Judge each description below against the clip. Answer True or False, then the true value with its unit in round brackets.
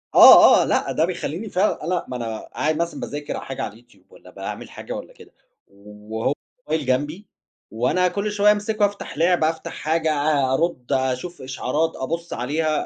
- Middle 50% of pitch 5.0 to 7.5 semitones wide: True (5.3 semitones)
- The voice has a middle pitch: True (155 Hz)